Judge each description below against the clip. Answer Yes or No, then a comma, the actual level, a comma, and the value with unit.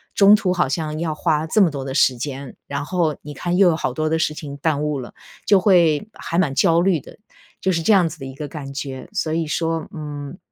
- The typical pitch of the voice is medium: Yes, medium, 155 Hz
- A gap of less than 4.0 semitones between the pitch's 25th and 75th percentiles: Yes, average, 3.3 semitones